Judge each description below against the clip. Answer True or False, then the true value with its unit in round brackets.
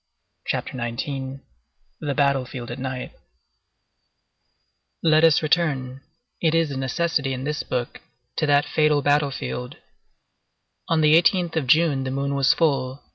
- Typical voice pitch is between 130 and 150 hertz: True (140 Hz)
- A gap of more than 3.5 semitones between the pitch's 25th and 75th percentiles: False (2.9 semitones)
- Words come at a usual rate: False (130 wpm)